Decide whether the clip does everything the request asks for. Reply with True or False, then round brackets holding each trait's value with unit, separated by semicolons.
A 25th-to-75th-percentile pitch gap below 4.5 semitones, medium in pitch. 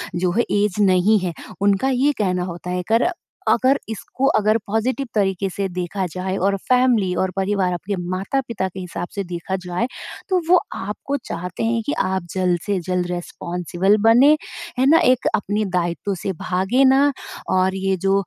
False (4.1 semitones; 195 Hz)